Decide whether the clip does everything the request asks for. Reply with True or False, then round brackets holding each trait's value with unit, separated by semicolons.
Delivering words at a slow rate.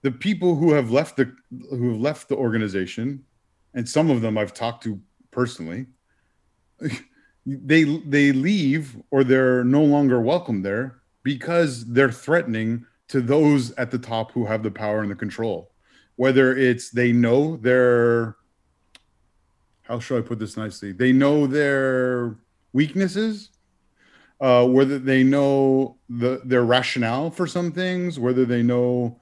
False (145 wpm)